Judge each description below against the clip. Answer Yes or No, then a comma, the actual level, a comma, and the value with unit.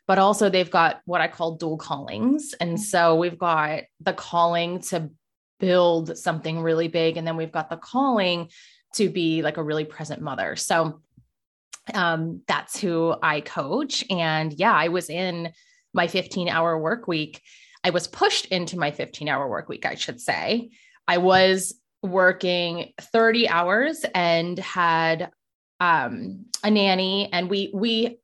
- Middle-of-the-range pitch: Yes, medium, 175 Hz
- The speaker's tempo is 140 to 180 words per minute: Yes, average, 155 wpm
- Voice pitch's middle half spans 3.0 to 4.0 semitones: Yes, average, 3.3 semitones